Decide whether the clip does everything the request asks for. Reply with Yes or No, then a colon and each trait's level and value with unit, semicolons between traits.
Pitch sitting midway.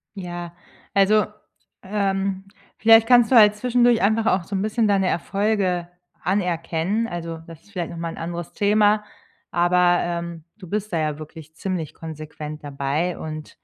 Yes: medium, 180 Hz